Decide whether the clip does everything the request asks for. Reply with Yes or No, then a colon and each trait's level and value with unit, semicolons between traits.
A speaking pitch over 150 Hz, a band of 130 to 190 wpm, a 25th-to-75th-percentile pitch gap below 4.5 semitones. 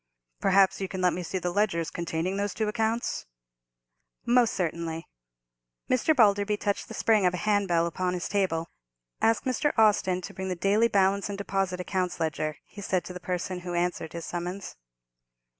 Yes: high, 190 Hz; average, 175 wpm; narrow, 2.6 semitones